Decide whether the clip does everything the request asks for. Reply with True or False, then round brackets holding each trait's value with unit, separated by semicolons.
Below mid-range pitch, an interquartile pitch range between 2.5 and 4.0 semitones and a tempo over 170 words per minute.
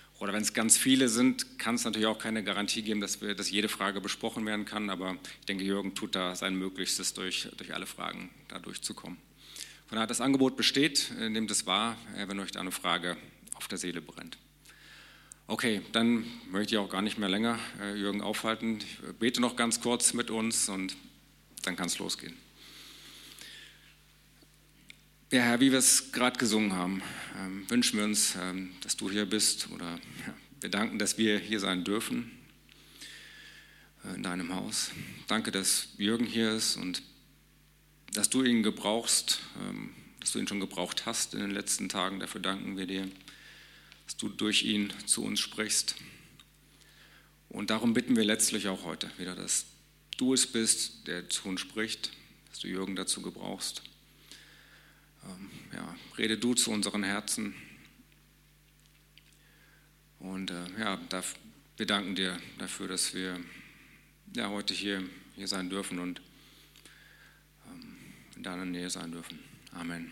False (105 Hz; 3.2 semitones; 155 wpm)